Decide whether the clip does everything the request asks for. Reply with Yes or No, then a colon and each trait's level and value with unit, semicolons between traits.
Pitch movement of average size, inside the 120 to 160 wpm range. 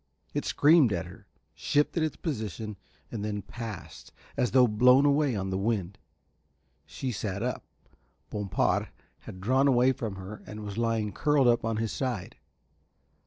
Yes: average, 4.1 semitones; average, 155 wpm